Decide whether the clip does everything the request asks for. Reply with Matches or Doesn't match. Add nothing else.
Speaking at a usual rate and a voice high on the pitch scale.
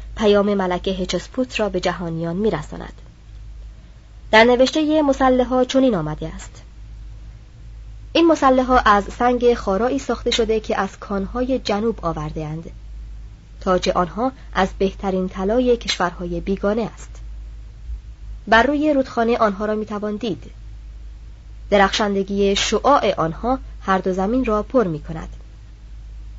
Matches